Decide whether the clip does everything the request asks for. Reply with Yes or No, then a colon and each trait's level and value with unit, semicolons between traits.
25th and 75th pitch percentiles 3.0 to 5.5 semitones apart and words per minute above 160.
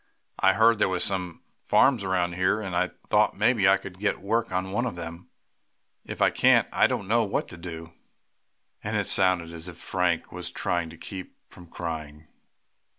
No: narrow, 2.5 semitones; average, 190 wpm